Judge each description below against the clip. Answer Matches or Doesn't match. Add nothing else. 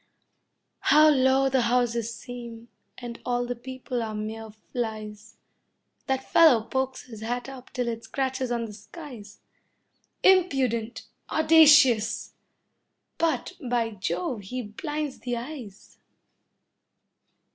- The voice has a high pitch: Matches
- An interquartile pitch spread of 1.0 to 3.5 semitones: Matches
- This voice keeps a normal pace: Doesn't match